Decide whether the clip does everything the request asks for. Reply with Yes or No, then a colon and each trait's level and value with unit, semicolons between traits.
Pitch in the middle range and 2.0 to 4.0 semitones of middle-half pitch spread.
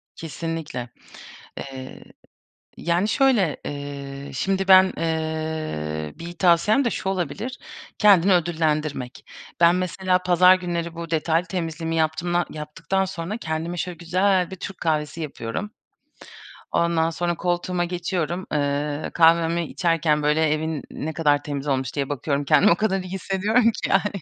Yes: medium, 165 Hz; average, 3.2 semitones